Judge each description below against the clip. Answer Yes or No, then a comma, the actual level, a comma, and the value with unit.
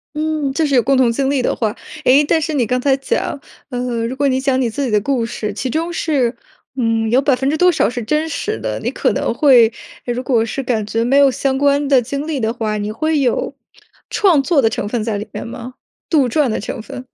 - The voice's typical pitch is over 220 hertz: Yes, very high, 260 Hz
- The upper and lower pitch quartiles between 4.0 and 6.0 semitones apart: No, average, 3.5 semitones